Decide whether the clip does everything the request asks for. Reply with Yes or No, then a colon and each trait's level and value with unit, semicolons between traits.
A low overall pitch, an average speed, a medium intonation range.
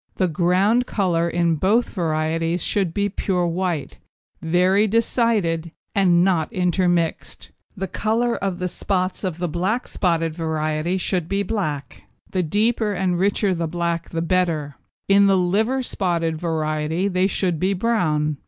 No: medium, 180 Hz; average, 145 wpm; average, 3.1 semitones